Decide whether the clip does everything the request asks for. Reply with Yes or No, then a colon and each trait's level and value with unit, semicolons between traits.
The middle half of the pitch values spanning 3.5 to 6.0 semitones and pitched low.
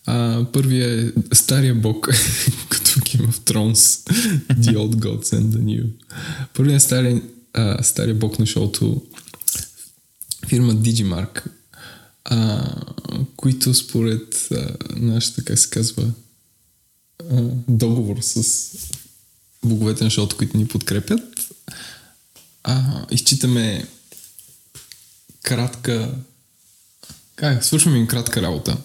No: average, 2.8 semitones; low, 120 Hz